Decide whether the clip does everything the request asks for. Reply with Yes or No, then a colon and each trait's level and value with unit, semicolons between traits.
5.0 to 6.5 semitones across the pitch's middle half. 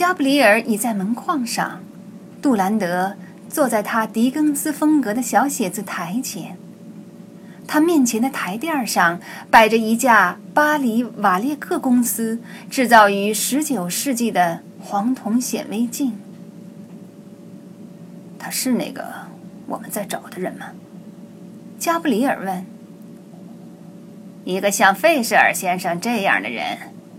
No: average, 4.4 semitones